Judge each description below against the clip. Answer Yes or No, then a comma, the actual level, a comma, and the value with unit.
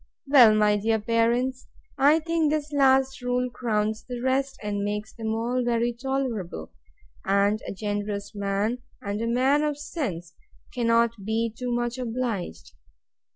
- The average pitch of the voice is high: Yes, high, 235 Hz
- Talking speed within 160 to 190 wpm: No, average, 145 wpm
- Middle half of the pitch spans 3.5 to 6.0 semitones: Yes, average, 3.8 semitones